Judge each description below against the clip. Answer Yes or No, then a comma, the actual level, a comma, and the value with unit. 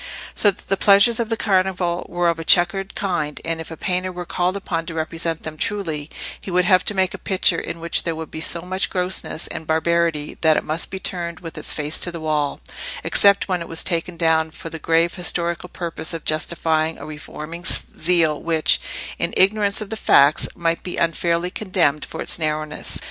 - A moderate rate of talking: No, fast, 210 wpm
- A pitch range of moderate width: No, narrow, 2.3 semitones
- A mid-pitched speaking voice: Yes, medium, 170 Hz